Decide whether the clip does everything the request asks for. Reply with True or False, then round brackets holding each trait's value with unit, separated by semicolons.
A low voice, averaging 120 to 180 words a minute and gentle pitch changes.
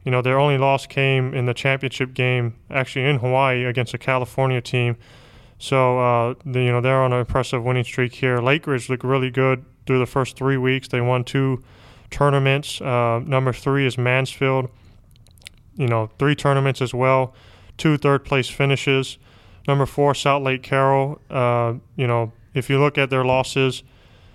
True (130 Hz; 175 wpm; 1.7 semitones)